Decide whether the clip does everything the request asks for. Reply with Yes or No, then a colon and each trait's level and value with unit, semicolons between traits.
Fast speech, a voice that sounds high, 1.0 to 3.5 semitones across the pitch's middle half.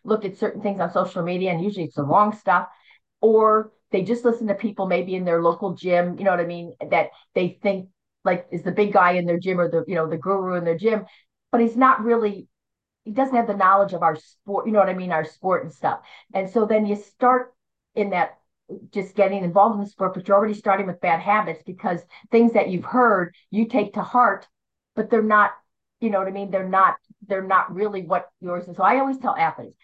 Yes: fast, 240 wpm; high, 195 Hz; average, 3.2 semitones